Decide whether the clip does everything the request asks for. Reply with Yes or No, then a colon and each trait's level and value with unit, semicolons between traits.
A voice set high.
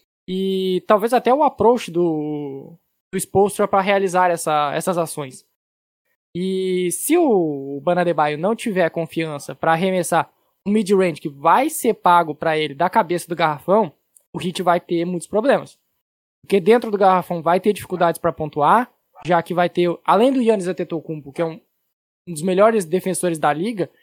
No: medium, 175 Hz